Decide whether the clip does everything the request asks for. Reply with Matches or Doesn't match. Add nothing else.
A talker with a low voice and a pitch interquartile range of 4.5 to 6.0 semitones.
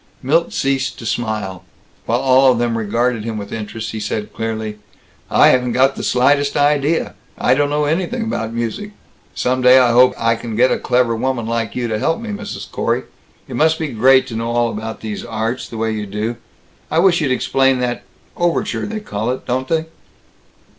Doesn't match